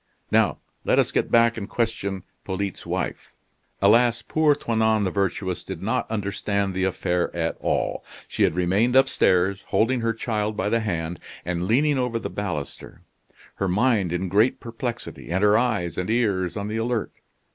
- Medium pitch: No, low, 105 Hz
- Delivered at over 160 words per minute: Yes, average, 170 wpm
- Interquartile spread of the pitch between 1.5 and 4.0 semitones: Yes, average, 3.7 semitones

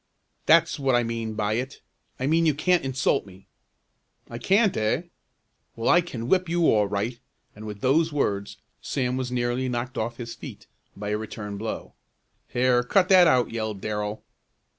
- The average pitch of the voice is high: No, low, 120 Hz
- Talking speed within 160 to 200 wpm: Yes, average, 175 wpm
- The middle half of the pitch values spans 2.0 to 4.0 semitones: No, average, 5.0 semitones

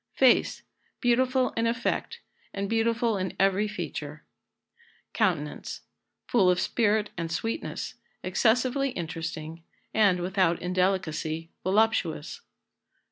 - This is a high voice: Yes, high, 195 Hz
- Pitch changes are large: No, average, 4.8 semitones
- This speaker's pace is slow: Yes, slow, 95 wpm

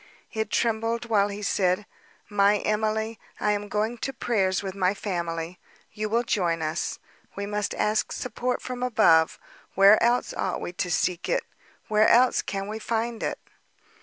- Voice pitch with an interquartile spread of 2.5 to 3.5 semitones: Yes, average, 2.9 semitones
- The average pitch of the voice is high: Yes, high, 210 Hz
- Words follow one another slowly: No, average, 160 wpm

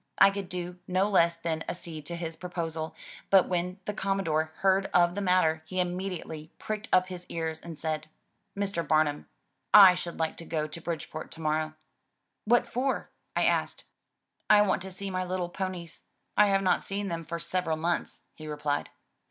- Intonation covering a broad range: No, average, 2.9 semitones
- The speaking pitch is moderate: Yes, medium, 175 Hz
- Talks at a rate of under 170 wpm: No, average, 185 wpm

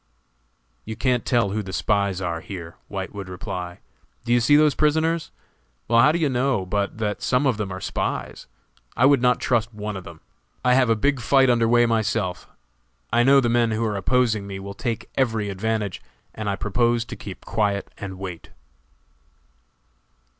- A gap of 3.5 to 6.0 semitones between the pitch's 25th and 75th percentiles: Yes, average, 3.8 semitones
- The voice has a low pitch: Yes, low, 110 Hz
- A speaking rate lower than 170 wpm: No, average, 185 wpm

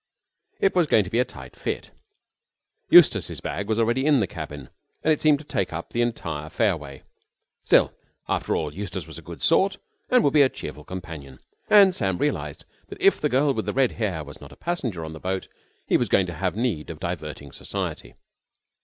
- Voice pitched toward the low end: Yes, very low, 95 Hz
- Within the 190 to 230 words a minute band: Yes, fast, 205 wpm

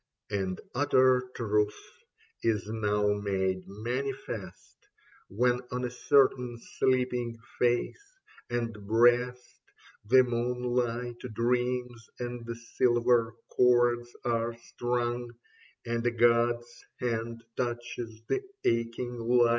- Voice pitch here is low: Yes, low, 120 Hz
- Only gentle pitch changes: Yes, narrow, 1.2 semitones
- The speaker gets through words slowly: Yes, slow, 95 wpm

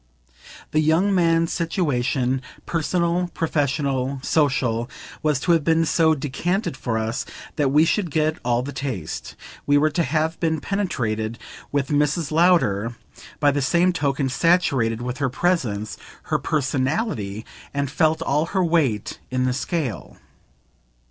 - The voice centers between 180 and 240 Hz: No, medium, 145 Hz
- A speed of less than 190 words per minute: Yes, average, 140 wpm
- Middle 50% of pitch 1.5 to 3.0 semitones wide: No, average, 4.5 semitones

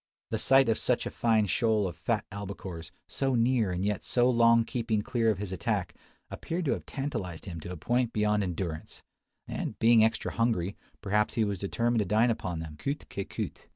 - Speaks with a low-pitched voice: Yes, low, 110 Hz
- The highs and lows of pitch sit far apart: No, average, 3.7 semitones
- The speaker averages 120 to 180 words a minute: No, average, 200 wpm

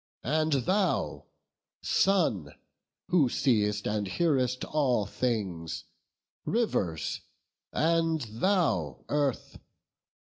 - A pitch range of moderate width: No, wide, 8.1 semitones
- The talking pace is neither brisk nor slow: No, slow, 75 wpm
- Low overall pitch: Yes, low, 130 Hz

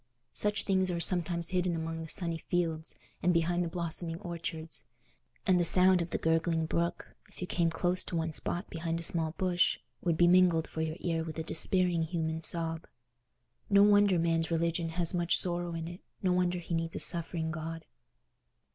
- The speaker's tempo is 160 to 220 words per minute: Yes, average, 190 wpm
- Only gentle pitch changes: Yes, narrow, 1.5 semitones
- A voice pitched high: No, medium, 170 Hz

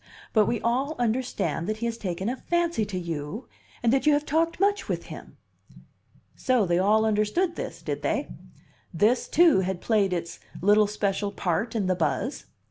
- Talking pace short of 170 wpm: No, average, 180 wpm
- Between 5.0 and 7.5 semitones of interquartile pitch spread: Yes, wide, 5.4 semitones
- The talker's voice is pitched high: Yes, high, 215 Hz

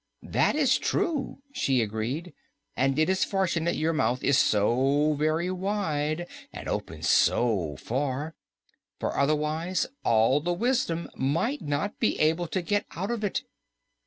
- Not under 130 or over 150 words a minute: Yes, average, 140 wpm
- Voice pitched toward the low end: No, medium, 155 Hz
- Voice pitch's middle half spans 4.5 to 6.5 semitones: Yes, wide, 5.4 semitones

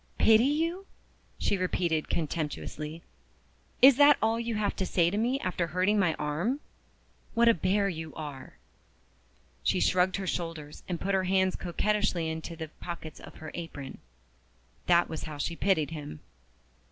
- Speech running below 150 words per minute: No, average, 155 wpm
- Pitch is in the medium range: Yes, medium, 180 Hz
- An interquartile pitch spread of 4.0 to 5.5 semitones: Yes, average, 4.5 semitones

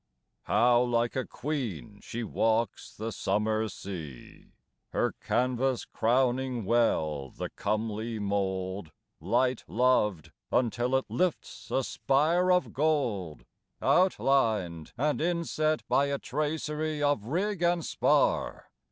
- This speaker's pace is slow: Yes, slow, 110 wpm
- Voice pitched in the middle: No, low, 120 Hz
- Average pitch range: No, wide, 5.8 semitones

